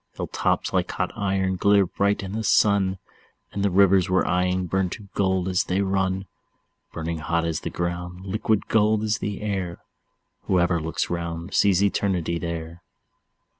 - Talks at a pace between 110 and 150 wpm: No, average, 165 wpm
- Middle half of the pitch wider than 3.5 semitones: No, narrow, 2.4 semitones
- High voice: No, very low, 95 Hz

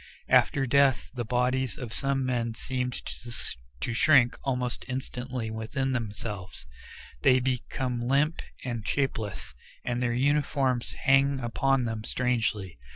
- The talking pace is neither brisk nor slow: No, slow, 120 wpm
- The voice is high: No, low, 125 Hz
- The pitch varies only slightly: Yes, narrow, 2.2 semitones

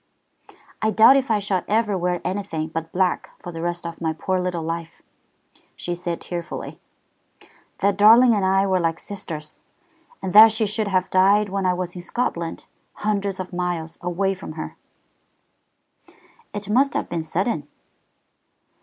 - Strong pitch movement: No, average, 3.2 semitones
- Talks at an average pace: Yes, average, 160 wpm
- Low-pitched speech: No, medium, 185 Hz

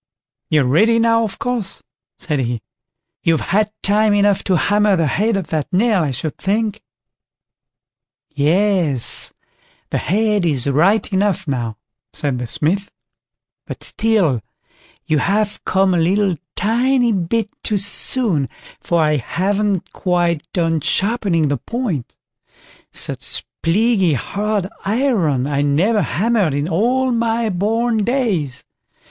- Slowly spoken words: Yes, slow, 130 wpm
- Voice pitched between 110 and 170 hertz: No, high, 195 Hz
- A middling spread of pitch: No, wide, 5.7 semitones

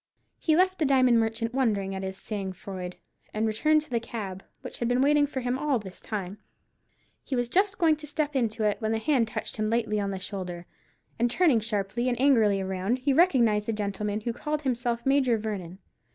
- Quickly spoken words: Yes, fast, 210 wpm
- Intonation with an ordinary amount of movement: Yes, average, 4.6 semitones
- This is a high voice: Yes, high, 230 Hz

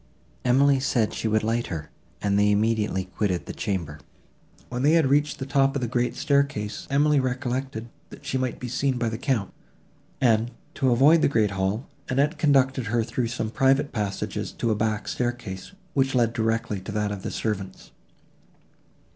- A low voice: Yes, low, 120 Hz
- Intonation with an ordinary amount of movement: Yes, average, 4.0 semitones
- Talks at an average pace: Yes, average, 180 wpm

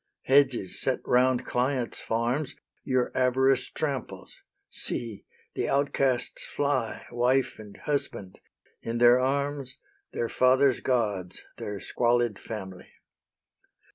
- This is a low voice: Yes, low, 125 Hz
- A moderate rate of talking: No, slow, 105 wpm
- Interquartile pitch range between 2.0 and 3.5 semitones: Yes, narrow, 2.5 semitones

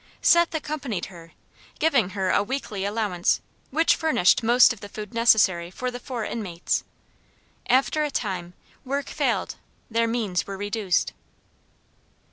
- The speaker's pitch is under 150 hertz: No, high, 220 Hz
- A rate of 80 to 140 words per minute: Yes, slow, 135 wpm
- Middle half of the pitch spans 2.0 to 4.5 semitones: No, average, 5.2 semitones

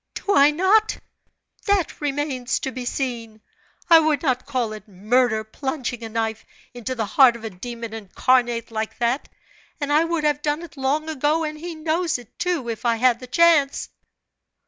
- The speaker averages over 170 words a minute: Yes, average, 180 wpm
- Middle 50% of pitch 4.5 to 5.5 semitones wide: Yes, average, 4.8 semitones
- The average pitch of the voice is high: Yes, very high, 260 Hz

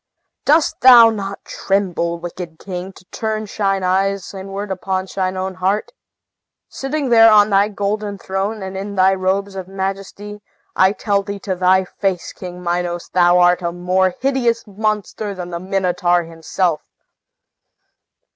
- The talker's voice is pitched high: Yes, high, 195 Hz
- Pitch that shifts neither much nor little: No, narrow, 2.1 semitones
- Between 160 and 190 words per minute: No, average, 145 wpm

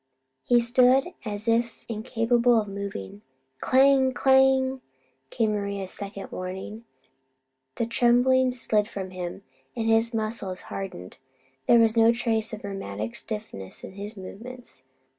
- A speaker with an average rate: No, slow, 125 wpm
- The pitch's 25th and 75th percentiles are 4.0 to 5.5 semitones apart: No, average, 3.5 semitones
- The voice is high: Yes, high, 225 Hz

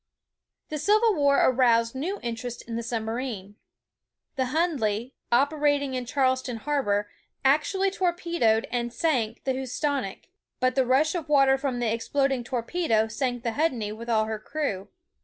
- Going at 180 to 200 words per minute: No, average, 145 wpm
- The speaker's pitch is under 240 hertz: No, very high, 255 Hz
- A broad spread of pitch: No, average, 4.1 semitones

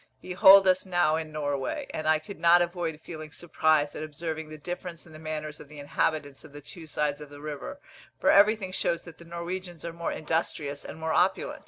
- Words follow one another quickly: Yes, fast, 210 wpm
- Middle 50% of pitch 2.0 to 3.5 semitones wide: Yes, narrow, 2.5 semitones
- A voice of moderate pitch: Yes, medium, 160 Hz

